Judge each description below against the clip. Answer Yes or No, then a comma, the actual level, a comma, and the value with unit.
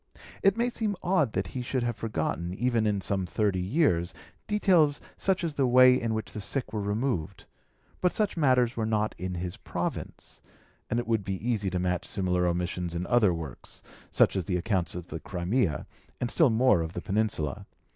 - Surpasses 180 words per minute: Yes, average, 195 wpm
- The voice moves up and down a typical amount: No, wide, 6.0 semitones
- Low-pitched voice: Yes, low, 110 Hz